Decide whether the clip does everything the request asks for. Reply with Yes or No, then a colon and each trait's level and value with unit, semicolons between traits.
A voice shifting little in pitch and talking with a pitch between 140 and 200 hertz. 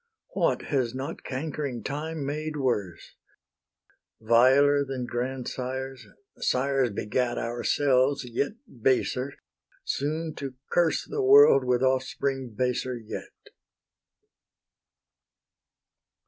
No: narrow, 2.3 semitones; low, 130 Hz